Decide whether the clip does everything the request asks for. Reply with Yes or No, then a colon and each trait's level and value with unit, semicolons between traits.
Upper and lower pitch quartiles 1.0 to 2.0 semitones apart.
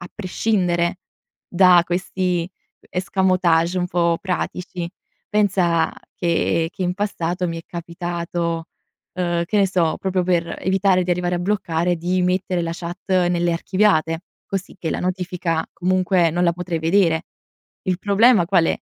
Yes: narrow, 1.6 semitones